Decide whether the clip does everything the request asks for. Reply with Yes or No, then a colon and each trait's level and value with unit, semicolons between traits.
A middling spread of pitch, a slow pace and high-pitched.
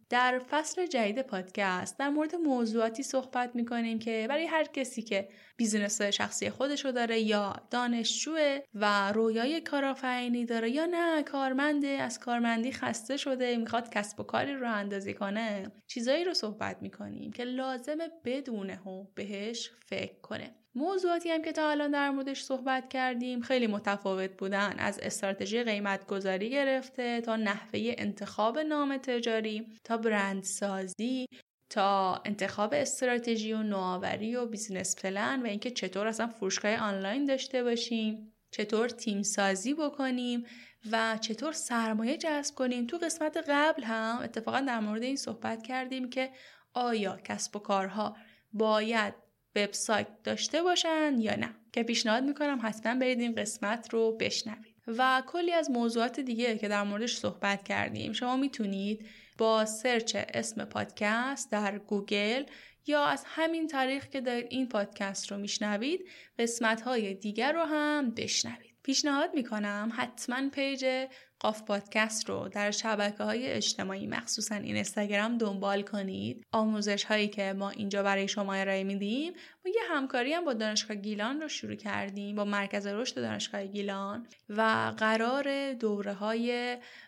No: average, 4.1 semitones; average, 145 wpm; high, 230 Hz